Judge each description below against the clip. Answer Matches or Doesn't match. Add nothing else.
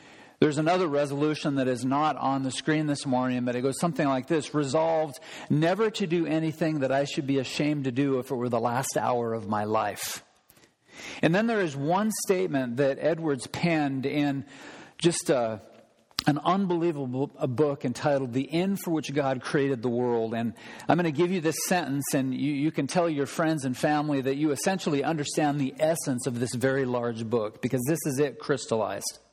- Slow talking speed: Doesn't match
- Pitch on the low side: Doesn't match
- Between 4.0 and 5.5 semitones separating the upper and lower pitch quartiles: Doesn't match